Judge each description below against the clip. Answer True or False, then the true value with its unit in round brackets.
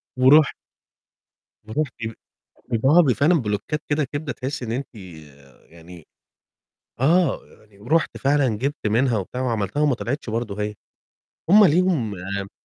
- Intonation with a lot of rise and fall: True (5.9 semitones)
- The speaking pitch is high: False (130 Hz)